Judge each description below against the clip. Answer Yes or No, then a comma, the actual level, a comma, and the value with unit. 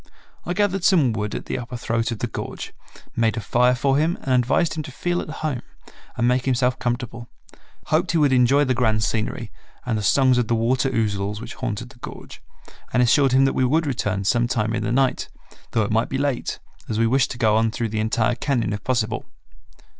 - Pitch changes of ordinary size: Yes, average, 3.0 semitones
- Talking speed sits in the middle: No, fast, 220 wpm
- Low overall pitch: Yes, low, 125 Hz